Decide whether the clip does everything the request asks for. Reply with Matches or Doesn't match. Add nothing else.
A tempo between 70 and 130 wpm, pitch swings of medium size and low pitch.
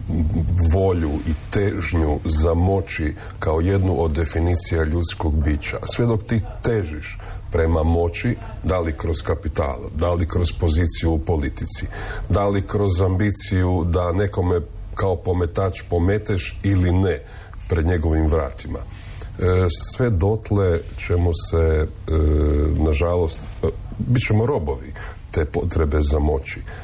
Matches